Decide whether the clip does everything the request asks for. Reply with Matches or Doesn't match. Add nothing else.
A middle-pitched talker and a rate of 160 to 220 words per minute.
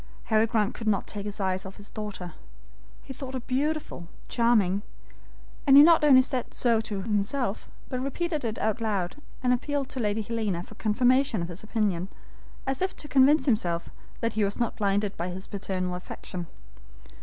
Doesn't match